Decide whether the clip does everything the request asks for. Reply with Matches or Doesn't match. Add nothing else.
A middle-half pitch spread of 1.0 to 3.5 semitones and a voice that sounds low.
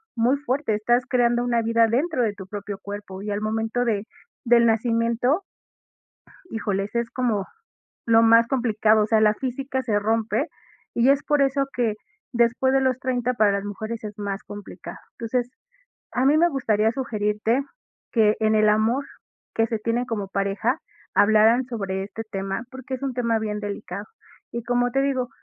Doesn't match